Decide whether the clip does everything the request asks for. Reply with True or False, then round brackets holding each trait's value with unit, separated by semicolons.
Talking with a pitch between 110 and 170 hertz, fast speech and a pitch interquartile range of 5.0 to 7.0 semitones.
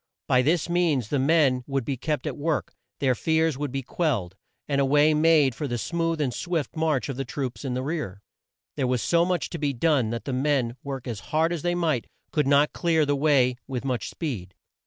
False (140 Hz; 220 wpm; 3.9 semitones)